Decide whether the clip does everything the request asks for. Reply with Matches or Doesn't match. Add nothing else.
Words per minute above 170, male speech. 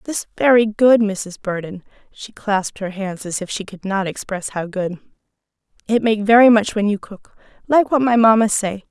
Doesn't match